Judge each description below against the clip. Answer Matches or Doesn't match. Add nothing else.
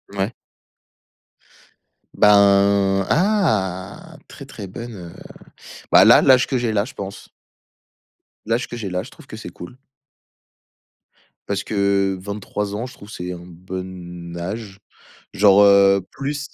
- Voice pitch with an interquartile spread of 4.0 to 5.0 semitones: Doesn't match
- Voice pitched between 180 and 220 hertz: Doesn't match